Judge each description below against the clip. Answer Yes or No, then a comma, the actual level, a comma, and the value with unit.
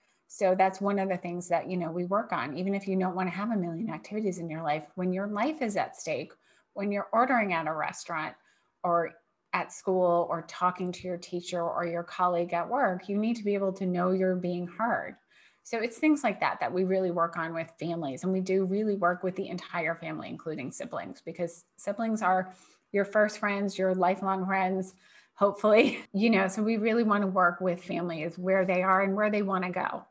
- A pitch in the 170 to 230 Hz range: Yes, medium, 185 Hz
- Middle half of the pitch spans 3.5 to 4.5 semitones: No, narrow, 2.5 semitones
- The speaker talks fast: Yes, fast, 225 wpm